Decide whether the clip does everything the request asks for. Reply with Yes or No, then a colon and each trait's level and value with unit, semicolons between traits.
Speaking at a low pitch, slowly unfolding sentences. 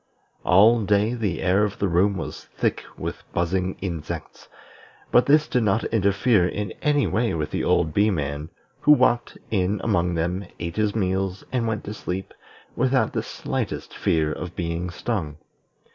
No: very low, 95 Hz; average, 165 wpm